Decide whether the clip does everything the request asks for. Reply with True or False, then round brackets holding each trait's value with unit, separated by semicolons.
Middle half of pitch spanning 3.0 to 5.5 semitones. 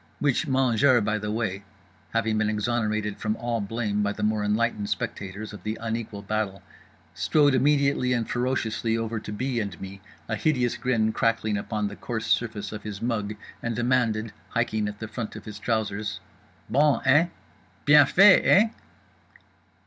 False (2.6 semitones)